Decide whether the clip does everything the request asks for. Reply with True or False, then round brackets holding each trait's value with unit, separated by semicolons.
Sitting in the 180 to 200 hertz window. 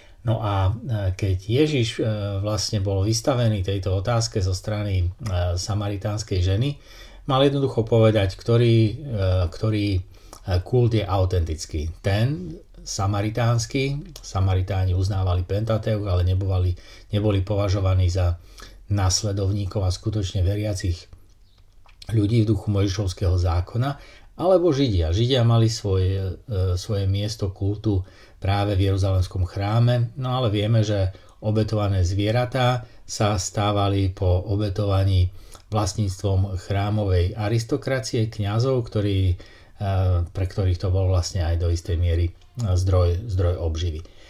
False (100 Hz)